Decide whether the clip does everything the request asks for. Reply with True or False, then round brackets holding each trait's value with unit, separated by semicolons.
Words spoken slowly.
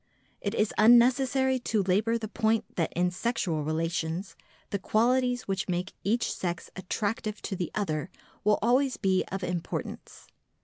False (145 wpm)